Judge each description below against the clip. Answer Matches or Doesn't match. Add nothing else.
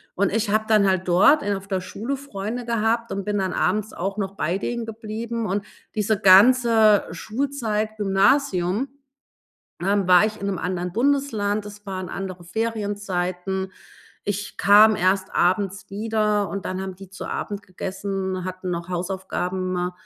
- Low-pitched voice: Doesn't match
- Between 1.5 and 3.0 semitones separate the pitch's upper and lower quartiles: Matches